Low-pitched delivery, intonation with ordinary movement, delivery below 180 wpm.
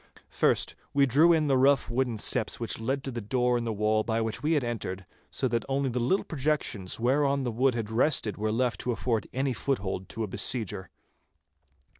No: low, 120 Hz; average, 3.4 semitones; average, 200 wpm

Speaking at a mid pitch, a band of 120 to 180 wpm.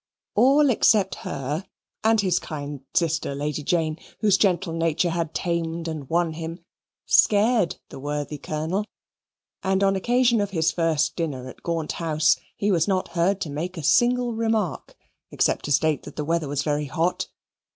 Yes: medium, 170 Hz; average, 165 wpm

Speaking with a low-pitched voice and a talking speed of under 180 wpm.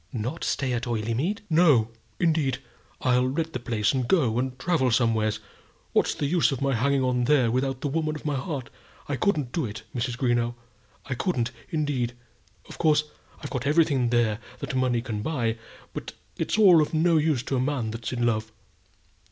No: low, 130 Hz; average, 185 wpm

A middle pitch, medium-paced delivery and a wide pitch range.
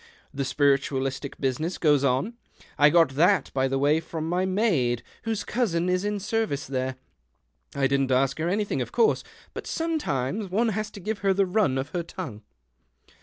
Yes: medium, 165 Hz; average, 180 wpm; wide, 6.9 semitones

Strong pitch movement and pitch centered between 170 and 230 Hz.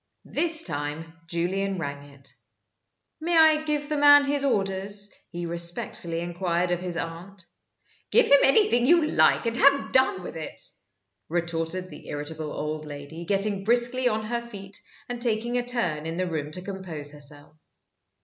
Yes: wide, 6.8 semitones; medium, 185 Hz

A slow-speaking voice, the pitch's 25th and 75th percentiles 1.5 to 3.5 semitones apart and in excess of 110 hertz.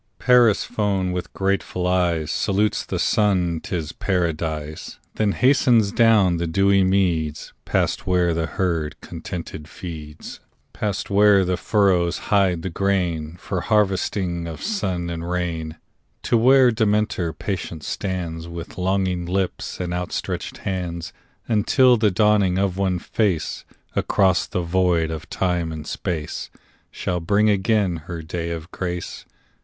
No: slow, 130 wpm; average, 2.8 semitones; very low, 90 Hz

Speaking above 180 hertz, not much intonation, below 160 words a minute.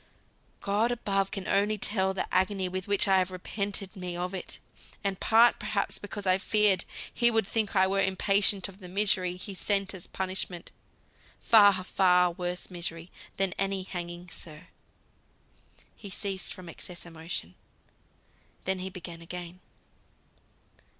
Yes: high, 190 Hz; narrow, 1.9 semitones; average, 145 wpm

